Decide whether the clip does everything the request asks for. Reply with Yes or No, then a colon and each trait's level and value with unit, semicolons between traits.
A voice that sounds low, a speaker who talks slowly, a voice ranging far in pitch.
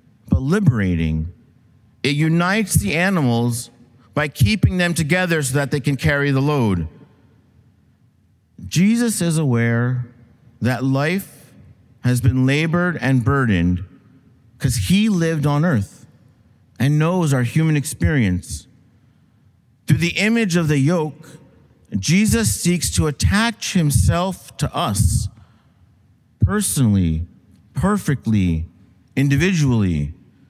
Yes: low, 130 Hz; slow, 105 wpm; wide, 6.1 semitones